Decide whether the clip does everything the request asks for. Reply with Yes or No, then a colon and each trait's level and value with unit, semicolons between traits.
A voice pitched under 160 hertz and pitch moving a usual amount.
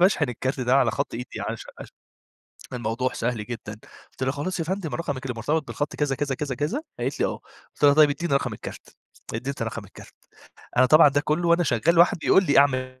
Yes: medium, 140 Hz; average, 3.7 semitones